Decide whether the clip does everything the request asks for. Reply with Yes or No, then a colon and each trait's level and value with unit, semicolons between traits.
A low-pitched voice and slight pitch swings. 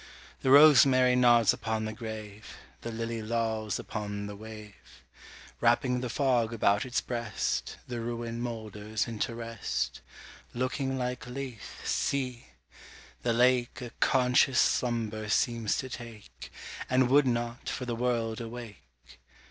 Yes: low, 115 Hz; narrow, 2.3 semitones